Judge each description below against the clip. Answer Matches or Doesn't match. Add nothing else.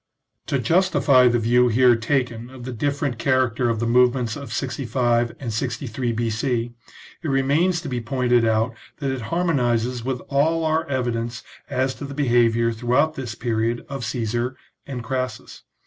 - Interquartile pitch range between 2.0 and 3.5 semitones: Matches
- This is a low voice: Matches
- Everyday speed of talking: Matches